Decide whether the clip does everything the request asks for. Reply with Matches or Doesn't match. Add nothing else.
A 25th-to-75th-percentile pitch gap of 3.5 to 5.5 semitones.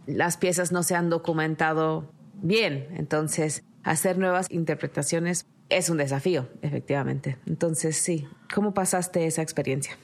Doesn't match